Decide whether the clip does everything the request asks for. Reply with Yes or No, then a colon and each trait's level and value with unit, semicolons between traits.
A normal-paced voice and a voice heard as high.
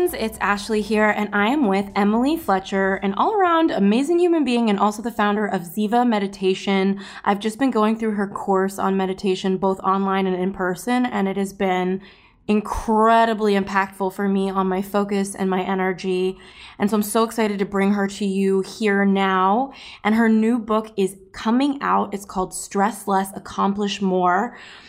Yes: average, 180 wpm; high, 200 Hz